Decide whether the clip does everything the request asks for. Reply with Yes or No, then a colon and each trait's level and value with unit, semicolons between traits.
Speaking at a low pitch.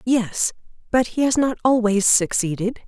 No: high, 225 Hz